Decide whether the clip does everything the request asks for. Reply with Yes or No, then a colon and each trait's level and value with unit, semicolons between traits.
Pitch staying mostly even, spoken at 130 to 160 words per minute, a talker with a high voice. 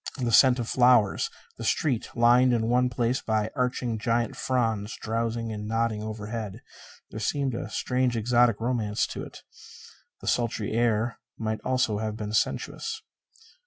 No: narrow, 2.2 semitones; average, 155 wpm; low, 115 Hz